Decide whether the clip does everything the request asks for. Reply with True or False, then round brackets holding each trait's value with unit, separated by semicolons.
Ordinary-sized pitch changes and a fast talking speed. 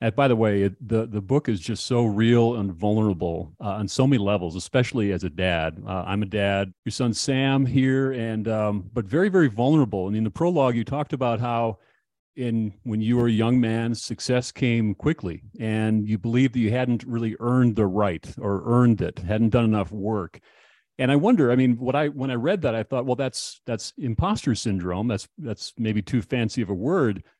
True (3.2 semitones; 215 wpm)